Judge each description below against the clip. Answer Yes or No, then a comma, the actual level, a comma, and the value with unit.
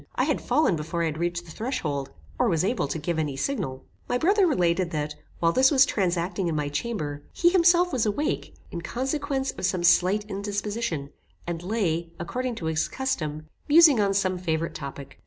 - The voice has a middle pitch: Yes, medium, 180 Hz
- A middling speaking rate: Yes, average, 190 wpm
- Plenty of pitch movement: Yes, wide, 7.7 semitones